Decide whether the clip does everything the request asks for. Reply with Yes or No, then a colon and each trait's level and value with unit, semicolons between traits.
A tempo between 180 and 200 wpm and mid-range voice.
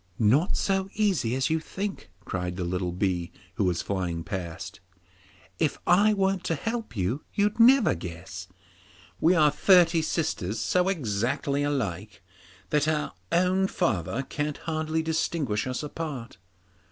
No: average, 140 wpm; medium, 145 Hz